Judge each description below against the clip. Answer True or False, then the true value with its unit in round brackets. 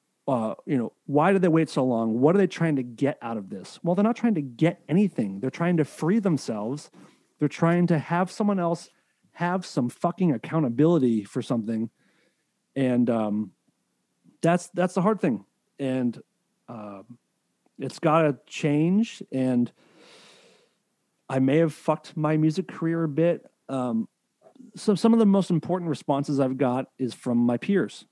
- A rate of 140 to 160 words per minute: False (170 wpm)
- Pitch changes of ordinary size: False (5.7 semitones)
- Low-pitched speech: False (155 Hz)